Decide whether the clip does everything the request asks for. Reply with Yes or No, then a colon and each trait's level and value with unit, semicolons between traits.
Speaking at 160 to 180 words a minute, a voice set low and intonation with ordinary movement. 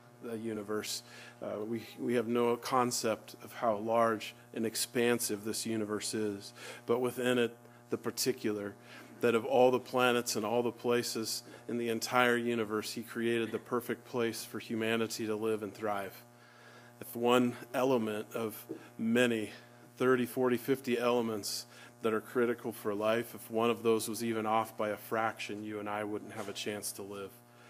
No: average, 170 wpm; low, 115 Hz; narrow, 1.6 semitones